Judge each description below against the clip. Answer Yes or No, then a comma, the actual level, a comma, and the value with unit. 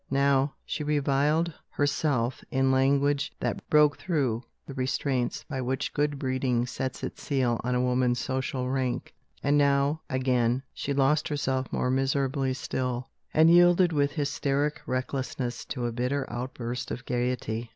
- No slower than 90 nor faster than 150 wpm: Yes, average, 145 wpm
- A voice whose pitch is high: No, low, 135 Hz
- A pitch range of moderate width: No, narrow, 2.2 semitones